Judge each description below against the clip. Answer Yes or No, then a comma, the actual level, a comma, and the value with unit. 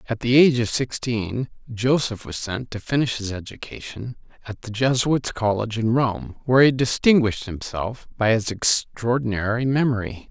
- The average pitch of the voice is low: Yes, low, 115 Hz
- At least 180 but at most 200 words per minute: No, average, 150 wpm